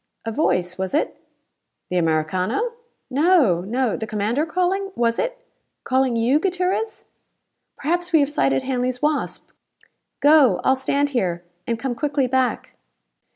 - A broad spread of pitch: Yes, wide, 6.2 semitones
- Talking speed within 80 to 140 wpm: Yes, slow, 135 wpm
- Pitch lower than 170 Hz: No, very high, 260 Hz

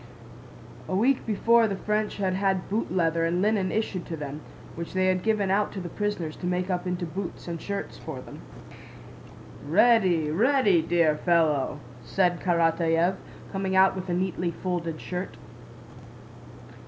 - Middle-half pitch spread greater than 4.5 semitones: No, average, 2.8 semitones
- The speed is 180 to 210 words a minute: No, average, 155 wpm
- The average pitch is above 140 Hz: Yes, medium, 185 Hz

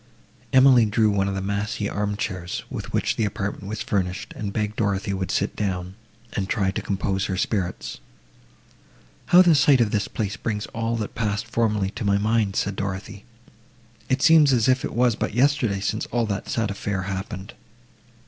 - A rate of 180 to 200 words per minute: Yes, average, 185 wpm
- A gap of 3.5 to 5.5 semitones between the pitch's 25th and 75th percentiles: No, narrow, 2.6 semitones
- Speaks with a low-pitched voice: Yes, low, 105 Hz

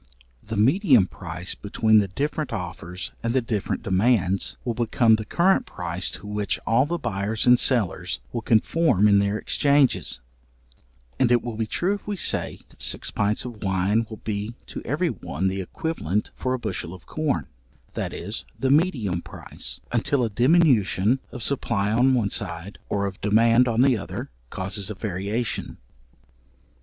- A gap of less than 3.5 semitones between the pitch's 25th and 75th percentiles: No, average, 4.3 semitones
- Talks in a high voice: No, low, 110 Hz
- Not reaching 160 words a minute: No, average, 170 wpm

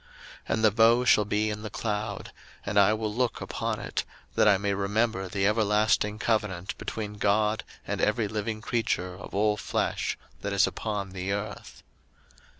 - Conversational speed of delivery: Yes, average, 170 wpm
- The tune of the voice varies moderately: No, narrow, 1.4 semitones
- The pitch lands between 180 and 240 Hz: No, low, 105 Hz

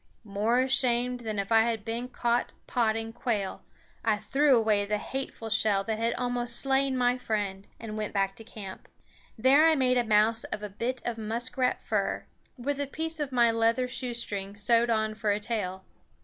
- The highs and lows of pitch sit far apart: No, average, 2.8 semitones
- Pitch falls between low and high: No, high, 230 Hz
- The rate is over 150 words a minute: Yes, average, 185 wpm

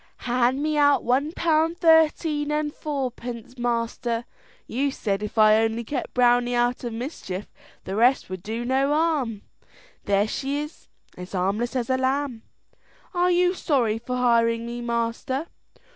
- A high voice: Yes, high, 245 Hz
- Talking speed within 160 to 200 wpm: No, average, 150 wpm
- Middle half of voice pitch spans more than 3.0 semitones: Yes, average, 3.9 semitones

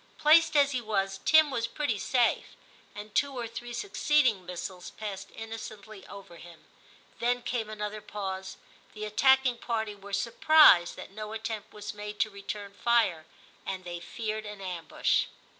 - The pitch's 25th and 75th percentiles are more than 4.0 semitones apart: No, average, 3.4 semitones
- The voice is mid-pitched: No, high, 215 Hz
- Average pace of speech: Yes, average, 155 wpm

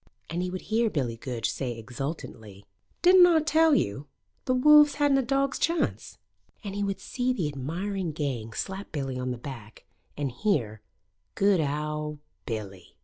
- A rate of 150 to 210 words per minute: Yes, average, 160 wpm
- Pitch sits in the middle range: Yes, medium, 155 Hz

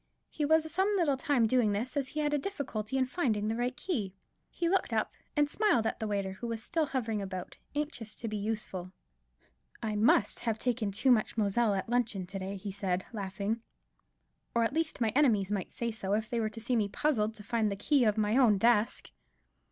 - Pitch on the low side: No, high, 225 Hz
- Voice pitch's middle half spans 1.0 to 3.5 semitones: No, average, 4.2 semitones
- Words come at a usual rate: No, fast, 215 wpm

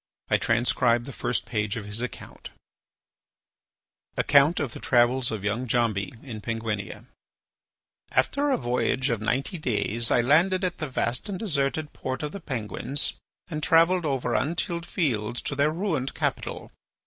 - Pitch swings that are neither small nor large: Yes, average, 5.0 semitones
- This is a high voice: No, low, 130 Hz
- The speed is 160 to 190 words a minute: No, average, 150 wpm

